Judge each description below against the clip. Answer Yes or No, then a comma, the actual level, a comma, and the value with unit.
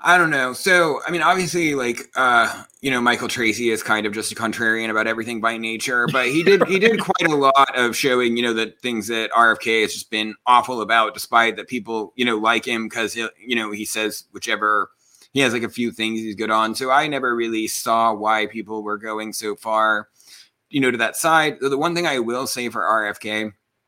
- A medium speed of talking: No, fast, 230 wpm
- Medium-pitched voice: No, low, 115 Hz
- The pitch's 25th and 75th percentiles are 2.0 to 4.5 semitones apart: Yes, narrow, 2.6 semitones